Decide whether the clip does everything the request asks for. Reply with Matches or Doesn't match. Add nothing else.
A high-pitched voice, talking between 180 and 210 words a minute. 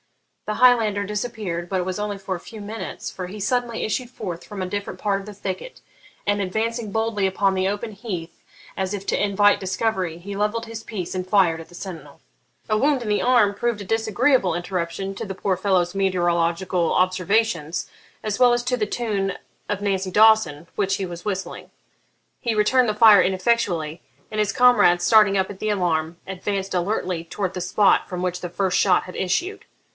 Matches